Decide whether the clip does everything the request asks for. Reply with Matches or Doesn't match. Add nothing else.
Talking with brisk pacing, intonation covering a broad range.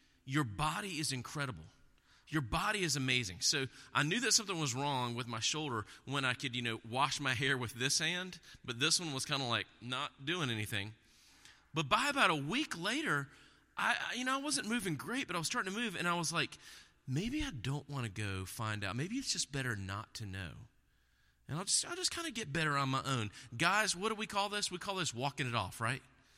Matches